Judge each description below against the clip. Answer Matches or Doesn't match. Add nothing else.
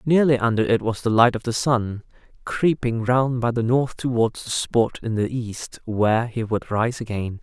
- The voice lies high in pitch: Doesn't match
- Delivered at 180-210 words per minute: Matches